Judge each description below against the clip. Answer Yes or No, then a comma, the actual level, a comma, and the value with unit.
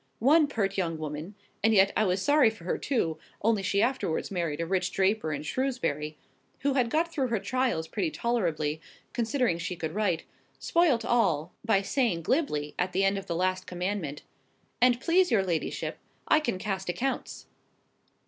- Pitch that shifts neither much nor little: No, wide, 6.2 semitones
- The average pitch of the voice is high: Yes, high, 195 Hz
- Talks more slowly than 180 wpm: Yes, average, 165 wpm